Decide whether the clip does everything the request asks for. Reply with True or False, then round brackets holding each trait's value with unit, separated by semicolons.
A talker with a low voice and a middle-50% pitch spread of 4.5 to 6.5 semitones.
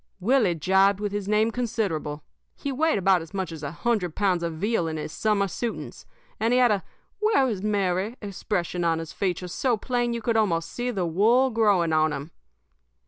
False (200 Hz; 5.1 semitones)